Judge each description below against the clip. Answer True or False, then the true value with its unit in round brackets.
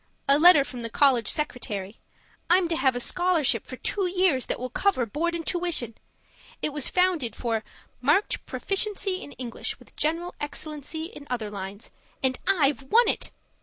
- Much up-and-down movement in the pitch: True (6.2 semitones)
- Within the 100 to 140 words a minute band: False (165 wpm)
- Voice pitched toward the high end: True (295 Hz)